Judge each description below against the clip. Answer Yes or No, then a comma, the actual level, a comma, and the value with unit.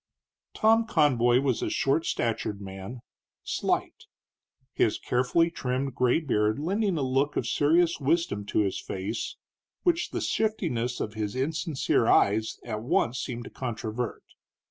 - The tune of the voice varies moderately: No, wide, 6.1 semitones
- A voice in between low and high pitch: No, low, 130 Hz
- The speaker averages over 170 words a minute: No, average, 140 wpm